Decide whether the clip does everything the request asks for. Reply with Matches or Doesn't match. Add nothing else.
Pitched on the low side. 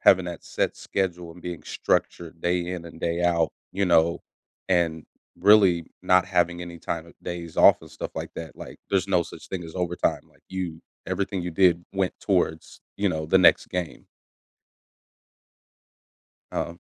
Matches